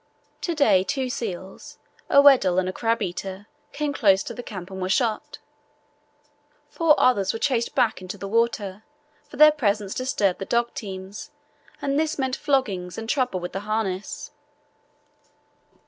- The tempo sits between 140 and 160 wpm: Yes, average, 155 wpm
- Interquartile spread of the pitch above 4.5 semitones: Yes, wide, 5.6 semitones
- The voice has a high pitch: Yes, high, 220 Hz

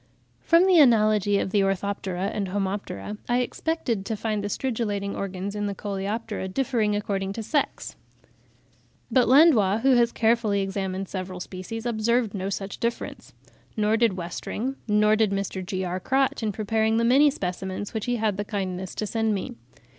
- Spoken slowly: No, average, 165 wpm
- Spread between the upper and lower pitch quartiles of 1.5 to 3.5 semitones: Yes, average, 3.0 semitones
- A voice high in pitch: Yes, high, 210 Hz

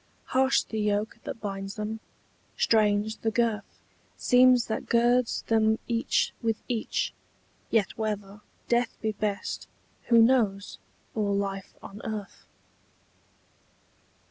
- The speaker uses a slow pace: Yes, slow, 115 wpm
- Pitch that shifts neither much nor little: No, narrow, 2.2 semitones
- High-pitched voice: Yes, high, 220 Hz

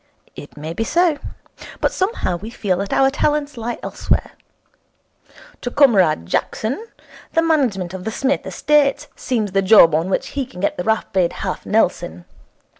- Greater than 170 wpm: No, average, 160 wpm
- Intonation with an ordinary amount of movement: No, wide, 7.3 semitones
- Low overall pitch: No, high, 220 Hz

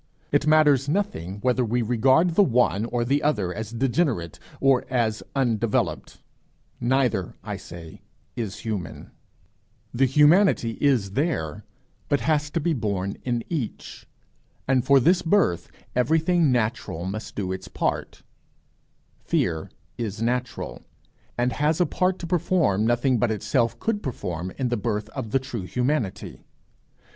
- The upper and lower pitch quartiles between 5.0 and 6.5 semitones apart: Yes, wide, 5.5 semitones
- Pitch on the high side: No, low, 125 Hz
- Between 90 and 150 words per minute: Yes, average, 140 wpm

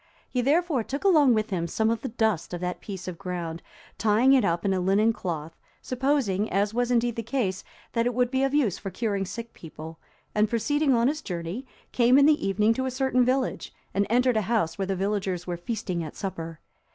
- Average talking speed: No, fast, 220 wpm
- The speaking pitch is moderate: No, high, 220 Hz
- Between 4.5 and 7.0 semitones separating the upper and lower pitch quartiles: Yes, average, 5.2 semitones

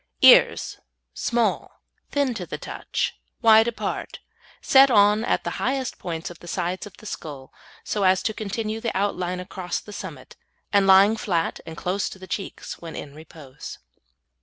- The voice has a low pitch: No, high, 195 Hz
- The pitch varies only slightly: No, average, 3.9 semitones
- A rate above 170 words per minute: No, average, 165 wpm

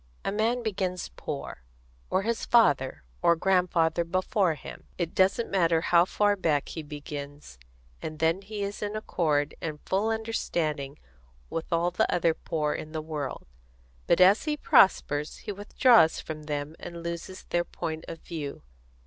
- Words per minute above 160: No, average, 155 wpm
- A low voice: No, medium, 170 Hz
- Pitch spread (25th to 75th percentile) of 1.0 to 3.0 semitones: No, average, 4.3 semitones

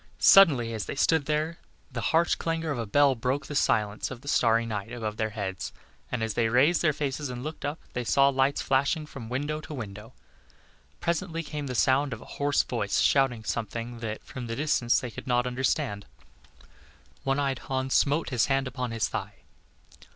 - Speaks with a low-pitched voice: Yes, low, 130 Hz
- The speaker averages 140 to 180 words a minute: No, average, 195 wpm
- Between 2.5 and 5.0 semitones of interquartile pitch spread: Yes, average, 3.9 semitones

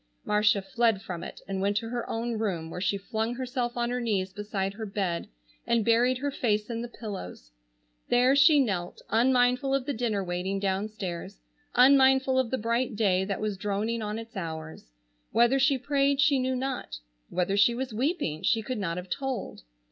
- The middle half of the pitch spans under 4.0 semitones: No, average, 4.4 semitones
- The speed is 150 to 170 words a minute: No, average, 185 wpm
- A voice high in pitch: Yes, high, 225 Hz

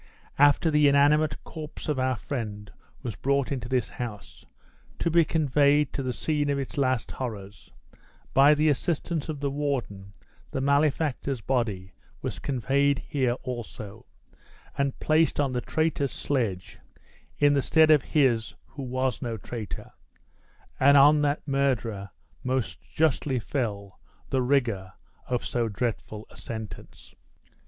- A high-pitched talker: No, low, 135 Hz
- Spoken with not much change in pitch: No, average, 3.8 semitones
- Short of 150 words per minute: Yes, average, 140 wpm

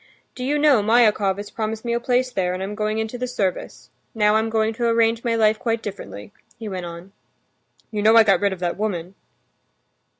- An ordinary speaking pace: No, fast, 210 wpm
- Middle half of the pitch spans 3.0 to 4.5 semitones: No, narrow, 2.6 semitones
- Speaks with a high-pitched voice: Yes, high, 220 Hz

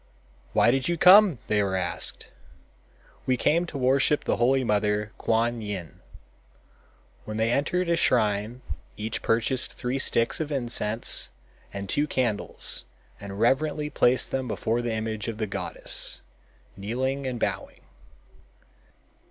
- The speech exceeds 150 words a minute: No, slow, 135 wpm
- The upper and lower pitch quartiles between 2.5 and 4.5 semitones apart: Yes, average, 4.0 semitones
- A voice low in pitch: Yes, low, 120 Hz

